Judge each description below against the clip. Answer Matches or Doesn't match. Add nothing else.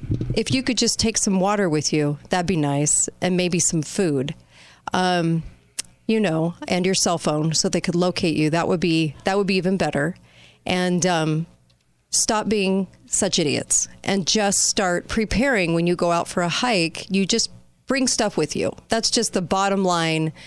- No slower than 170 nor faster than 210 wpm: Matches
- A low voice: Doesn't match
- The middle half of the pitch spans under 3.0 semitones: Doesn't match